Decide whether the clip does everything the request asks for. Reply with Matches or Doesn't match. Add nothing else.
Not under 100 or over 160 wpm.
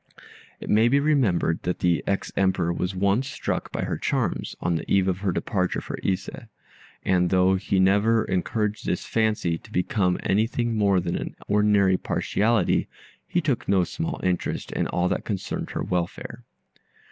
Doesn't match